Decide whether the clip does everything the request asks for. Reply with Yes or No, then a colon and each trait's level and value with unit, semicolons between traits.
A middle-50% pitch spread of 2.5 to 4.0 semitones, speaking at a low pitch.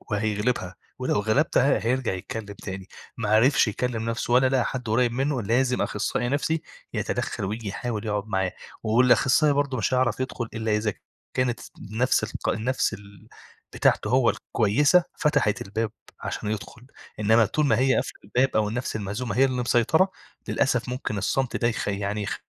Yes: average, 3.4 semitones; low, 115 Hz